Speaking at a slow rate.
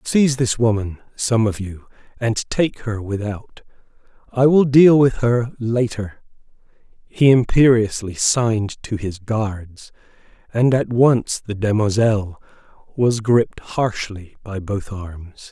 Yes: slow, 130 wpm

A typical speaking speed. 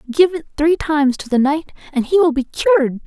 No: fast, 235 wpm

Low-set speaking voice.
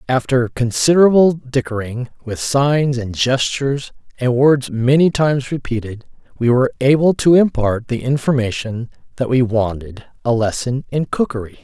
Yes: low, 130 Hz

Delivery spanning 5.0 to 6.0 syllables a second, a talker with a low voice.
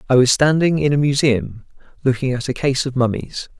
Yes: 5.4 syllables/s; low, 130 Hz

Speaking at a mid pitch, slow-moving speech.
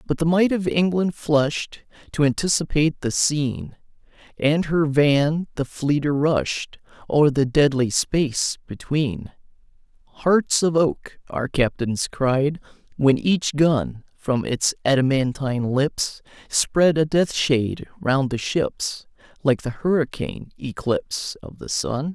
Yes: medium, 145 Hz; slow, 130 wpm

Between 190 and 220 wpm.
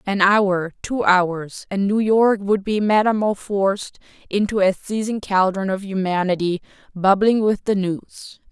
No: average, 140 wpm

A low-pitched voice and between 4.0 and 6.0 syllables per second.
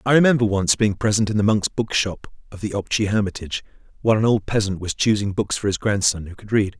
No: low, 105 Hz; 6.2 syllables/s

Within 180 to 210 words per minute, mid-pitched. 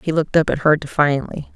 No: fast, 230 wpm; medium, 150 Hz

